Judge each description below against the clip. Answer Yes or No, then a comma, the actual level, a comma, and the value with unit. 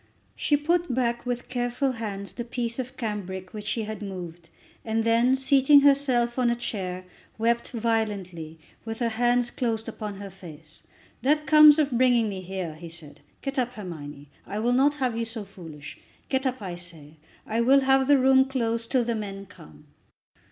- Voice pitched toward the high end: Yes, high, 230 Hz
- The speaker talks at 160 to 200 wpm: Yes, average, 180 wpm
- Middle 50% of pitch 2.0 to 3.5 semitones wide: No, average, 4.9 semitones